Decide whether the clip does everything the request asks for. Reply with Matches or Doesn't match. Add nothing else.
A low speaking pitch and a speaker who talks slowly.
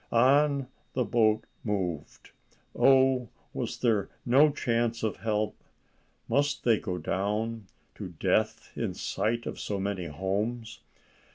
Matches